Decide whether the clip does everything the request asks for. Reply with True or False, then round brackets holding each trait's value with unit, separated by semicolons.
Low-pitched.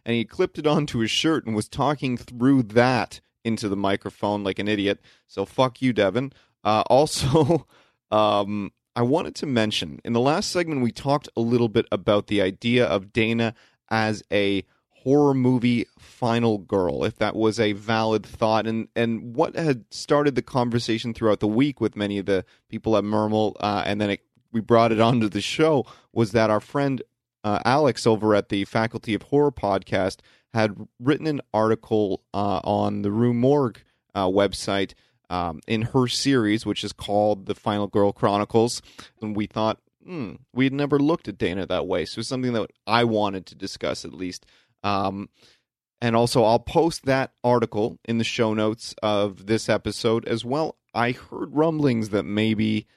True (110 Hz)